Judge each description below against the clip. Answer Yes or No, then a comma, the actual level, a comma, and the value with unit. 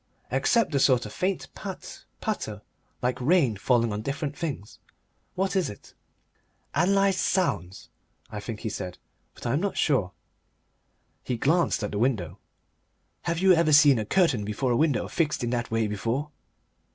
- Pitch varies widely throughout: Yes, wide, 7.4 semitones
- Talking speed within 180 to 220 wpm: No, average, 165 wpm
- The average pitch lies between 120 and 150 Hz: Yes, low, 135 Hz